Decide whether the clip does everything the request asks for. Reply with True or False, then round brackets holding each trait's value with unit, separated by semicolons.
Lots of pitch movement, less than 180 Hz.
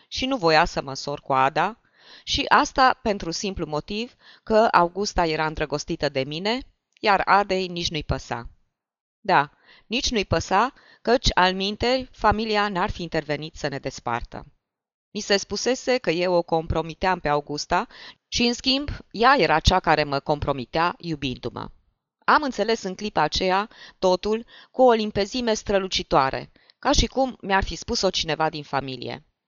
False (5.9 semitones; 185 Hz)